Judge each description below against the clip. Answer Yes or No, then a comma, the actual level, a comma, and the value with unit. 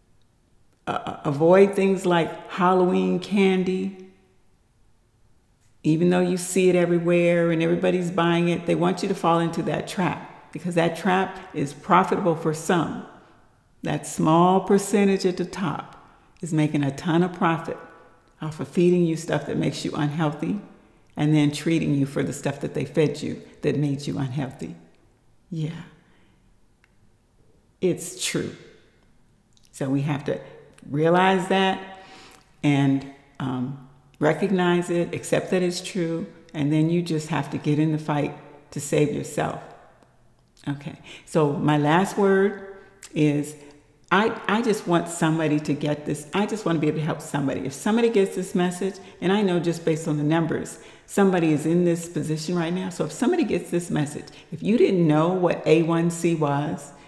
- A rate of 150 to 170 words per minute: Yes, average, 160 wpm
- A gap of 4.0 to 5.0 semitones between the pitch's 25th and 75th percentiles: No, average, 3.5 semitones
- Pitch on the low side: No, medium, 165 Hz